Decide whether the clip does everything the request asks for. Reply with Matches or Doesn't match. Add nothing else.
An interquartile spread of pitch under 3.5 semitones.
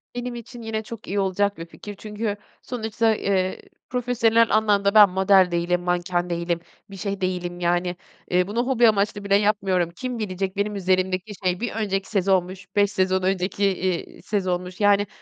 Matches